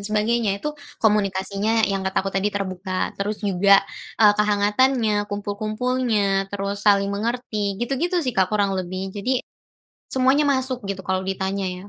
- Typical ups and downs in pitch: Yes, average, 3.1 semitones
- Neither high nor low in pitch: No, high, 205 Hz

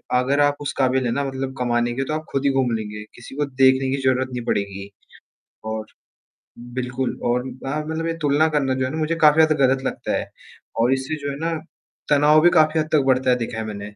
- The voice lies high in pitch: No, low, 135 Hz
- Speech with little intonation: No, average, 3.2 semitones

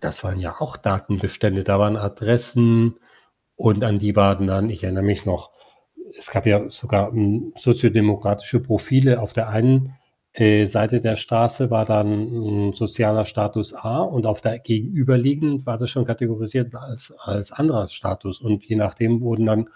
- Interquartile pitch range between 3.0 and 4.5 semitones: No, narrow, 2.5 semitones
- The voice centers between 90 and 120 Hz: Yes, low, 110 Hz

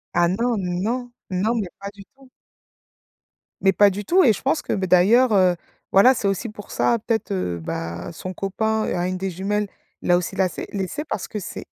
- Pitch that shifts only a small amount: No, average, 3.3 semitones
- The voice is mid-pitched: No, high, 195 Hz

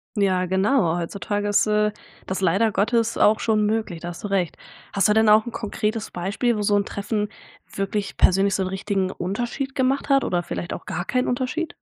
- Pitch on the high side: Yes, high, 205 Hz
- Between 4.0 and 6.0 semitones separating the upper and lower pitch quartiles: No, average, 2.8 semitones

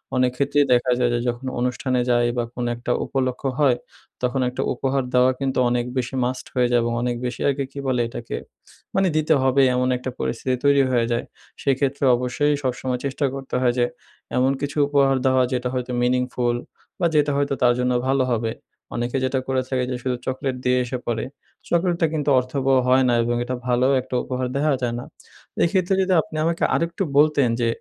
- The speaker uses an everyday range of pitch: No, narrow, 2.0 semitones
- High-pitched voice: No, low, 130 Hz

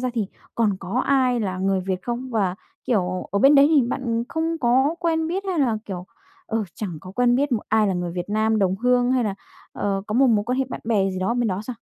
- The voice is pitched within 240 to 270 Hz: No, high, 230 Hz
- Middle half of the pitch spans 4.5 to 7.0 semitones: Yes, average, 4.8 semitones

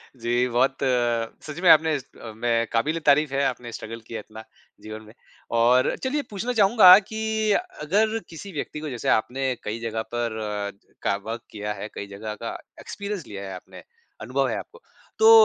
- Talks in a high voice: No, low, 125 Hz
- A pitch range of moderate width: No, wide, 6.6 semitones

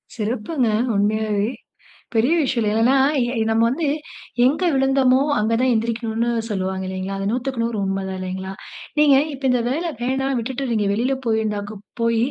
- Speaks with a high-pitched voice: Yes, high, 230 Hz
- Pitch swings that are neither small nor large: Yes, average, 3.8 semitones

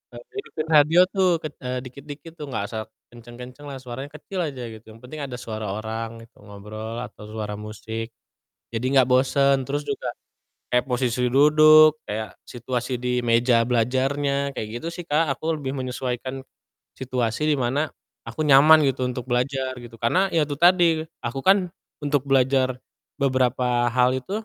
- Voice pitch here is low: Yes, low, 130 Hz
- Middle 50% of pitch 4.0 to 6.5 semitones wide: No, average, 3.4 semitones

